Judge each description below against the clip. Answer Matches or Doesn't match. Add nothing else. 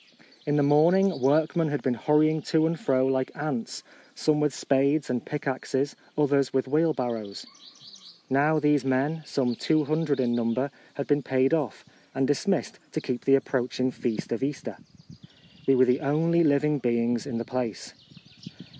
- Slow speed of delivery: Doesn't match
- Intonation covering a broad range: Doesn't match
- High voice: Doesn't match